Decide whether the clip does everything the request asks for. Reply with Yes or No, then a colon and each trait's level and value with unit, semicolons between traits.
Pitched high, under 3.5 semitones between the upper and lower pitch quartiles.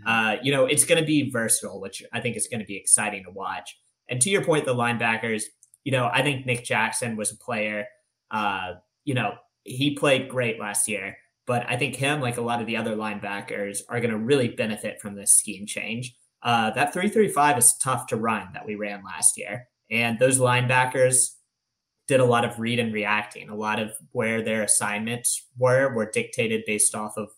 No: low, 120 Hz; average, 3.0 semitones